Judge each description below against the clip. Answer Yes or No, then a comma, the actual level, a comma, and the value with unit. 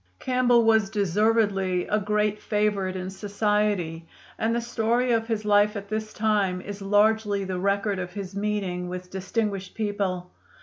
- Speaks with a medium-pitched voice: No, high, 205 Hz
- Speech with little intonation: Yes, narrow, 2.2 semitones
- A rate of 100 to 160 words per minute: Yes, average, 150 wpm